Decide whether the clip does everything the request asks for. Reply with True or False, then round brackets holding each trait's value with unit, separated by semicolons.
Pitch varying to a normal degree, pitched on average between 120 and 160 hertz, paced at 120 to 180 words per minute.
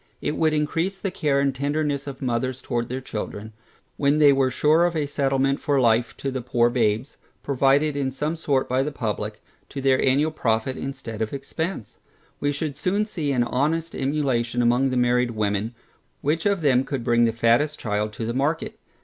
False (3.8 semitones; 135 Hz; 190 wpm)